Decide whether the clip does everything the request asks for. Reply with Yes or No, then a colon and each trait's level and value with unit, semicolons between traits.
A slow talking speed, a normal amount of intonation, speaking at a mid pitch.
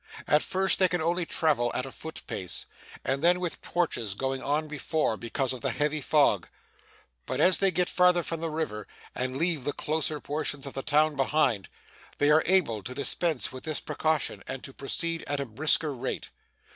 No: average, 195 wpm; average, 3.7 semitones; medium, 150 Hz